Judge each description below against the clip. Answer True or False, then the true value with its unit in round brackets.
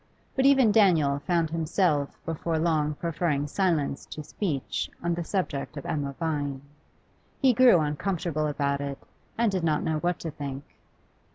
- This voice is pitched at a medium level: True (160 Hz)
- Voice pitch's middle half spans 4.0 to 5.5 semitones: False (3.6 semitones)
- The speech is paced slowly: False (155 wpm)